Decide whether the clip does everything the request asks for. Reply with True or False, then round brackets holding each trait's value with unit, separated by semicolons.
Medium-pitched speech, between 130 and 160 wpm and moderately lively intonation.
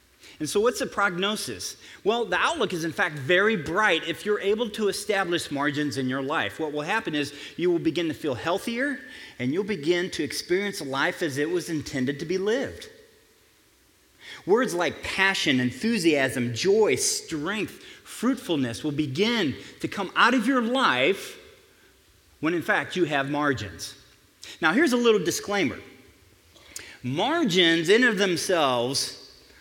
False (180 Hz; 150 wpm; 7.3 semitones)